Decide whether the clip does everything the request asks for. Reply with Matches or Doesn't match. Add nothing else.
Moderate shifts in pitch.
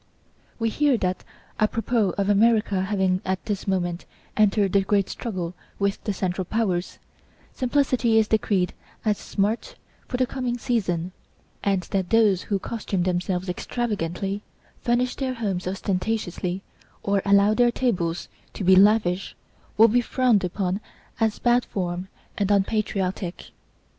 Matches